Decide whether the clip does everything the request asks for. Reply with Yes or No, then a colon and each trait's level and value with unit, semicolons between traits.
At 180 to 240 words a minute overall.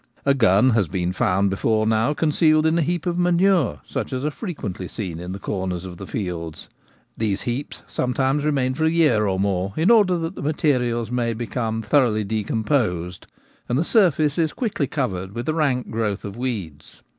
Yes: average, 190 wpm